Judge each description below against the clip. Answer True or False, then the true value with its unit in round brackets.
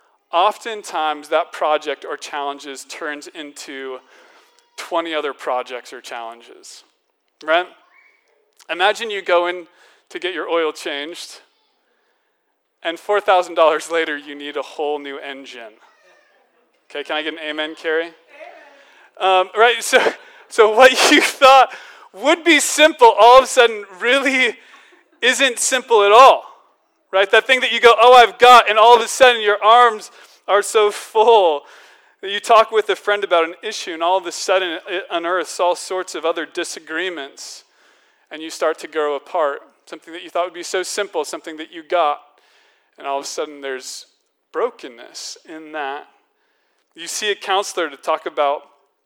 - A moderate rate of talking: True (160 wpm)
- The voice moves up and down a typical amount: False (8.3 semitones)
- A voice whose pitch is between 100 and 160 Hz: False (190 Hz)